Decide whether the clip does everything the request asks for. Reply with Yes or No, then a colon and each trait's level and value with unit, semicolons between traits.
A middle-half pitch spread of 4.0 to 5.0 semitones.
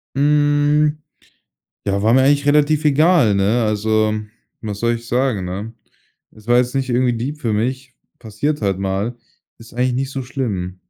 Yes: average, 4.7 semitones